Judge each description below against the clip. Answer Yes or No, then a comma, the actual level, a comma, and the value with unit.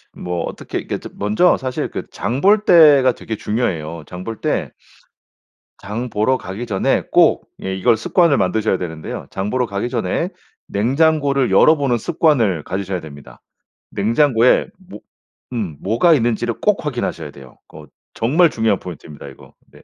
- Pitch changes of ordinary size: No, wide, 6.4 semitones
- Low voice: Yes, low, 115 Hz